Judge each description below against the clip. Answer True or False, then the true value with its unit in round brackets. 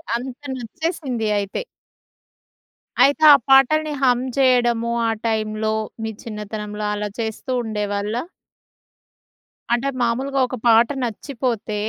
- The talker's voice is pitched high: True (235 Hz)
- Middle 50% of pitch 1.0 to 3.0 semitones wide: False (3.4 semitones)